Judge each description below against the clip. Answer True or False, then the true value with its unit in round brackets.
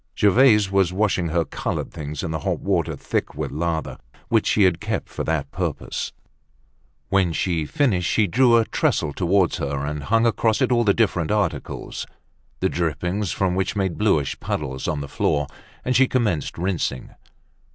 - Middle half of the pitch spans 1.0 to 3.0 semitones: False (5.1 semitones)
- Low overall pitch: True (90 Hz)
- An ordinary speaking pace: True (175 wpm)